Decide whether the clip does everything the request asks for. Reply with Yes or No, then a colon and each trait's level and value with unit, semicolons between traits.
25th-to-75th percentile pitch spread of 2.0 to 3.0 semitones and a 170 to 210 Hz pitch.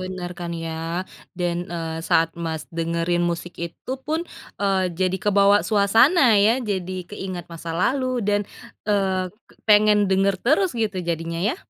No: average, 3.4 semitones; medium, 185 Hz